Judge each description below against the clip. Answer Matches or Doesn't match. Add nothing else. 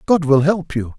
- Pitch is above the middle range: Doesn't match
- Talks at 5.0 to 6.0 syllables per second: Doesn't match